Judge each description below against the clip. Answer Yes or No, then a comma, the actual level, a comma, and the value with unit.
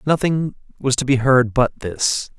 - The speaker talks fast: No, average, 175 wpm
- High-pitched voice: No, low, 130 Hz